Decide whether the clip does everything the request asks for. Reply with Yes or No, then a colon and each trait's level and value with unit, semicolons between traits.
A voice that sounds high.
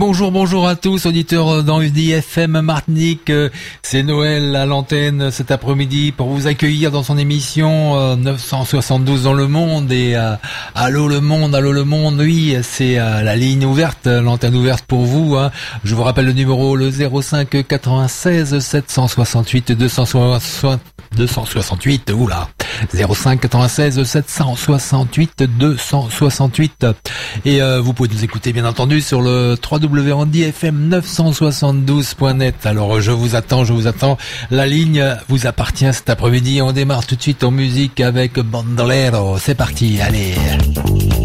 No: low, 135 Hz